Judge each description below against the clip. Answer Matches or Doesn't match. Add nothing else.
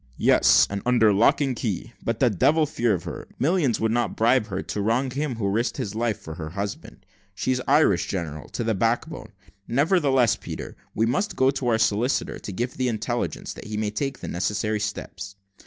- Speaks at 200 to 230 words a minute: Matches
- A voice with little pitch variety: Doesn't match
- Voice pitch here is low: Matches